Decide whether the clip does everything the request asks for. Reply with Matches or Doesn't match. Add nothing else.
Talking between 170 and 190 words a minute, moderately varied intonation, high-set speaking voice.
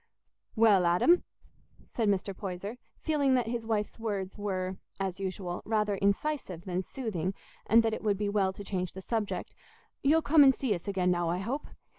Matches